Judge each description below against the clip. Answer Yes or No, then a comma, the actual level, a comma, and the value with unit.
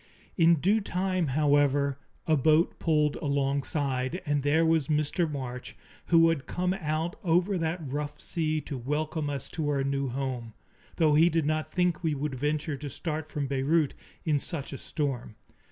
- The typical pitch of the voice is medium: Yes, medium, 150 Hz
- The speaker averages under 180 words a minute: Yes, average, 170 wpm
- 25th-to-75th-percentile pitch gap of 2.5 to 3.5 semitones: Yes, average, 2.8 semitones